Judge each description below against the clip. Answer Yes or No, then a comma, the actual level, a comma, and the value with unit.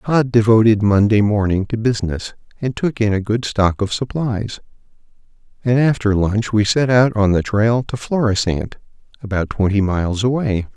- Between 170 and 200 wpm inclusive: No, average, 160 wpm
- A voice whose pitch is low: Yes, low, 110 Hz